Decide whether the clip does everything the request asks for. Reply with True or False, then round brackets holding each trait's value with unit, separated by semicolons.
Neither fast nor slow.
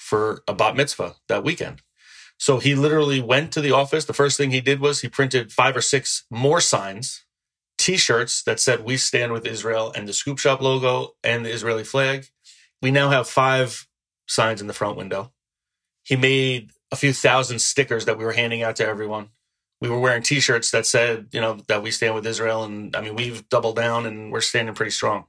False (215 wpm)